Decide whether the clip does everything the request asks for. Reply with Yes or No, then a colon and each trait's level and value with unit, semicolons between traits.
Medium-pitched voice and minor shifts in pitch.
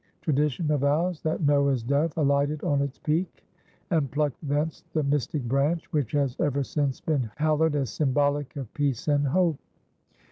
Yes: medium, 145 Hz; narrow, 1.8 semitones